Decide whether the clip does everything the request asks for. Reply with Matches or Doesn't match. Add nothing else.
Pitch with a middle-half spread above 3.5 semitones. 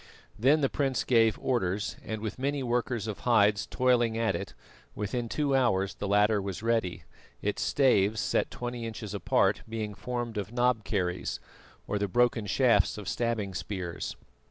Doesn't match